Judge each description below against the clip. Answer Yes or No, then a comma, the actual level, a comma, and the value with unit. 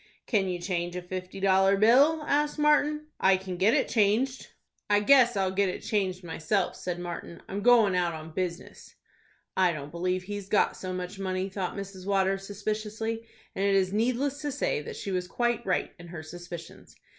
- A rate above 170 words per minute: Yes, average, 190 wpm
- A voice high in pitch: Yes, high, 195 Hz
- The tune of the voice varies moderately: Yes, average, 3.7 semitones